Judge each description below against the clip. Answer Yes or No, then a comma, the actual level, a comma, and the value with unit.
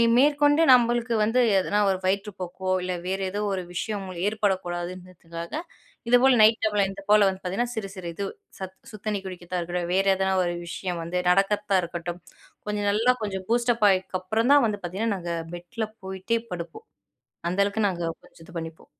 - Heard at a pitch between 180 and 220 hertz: Yes, high, 195 Hz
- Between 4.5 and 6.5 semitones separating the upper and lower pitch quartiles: No, average, 3.3 semitones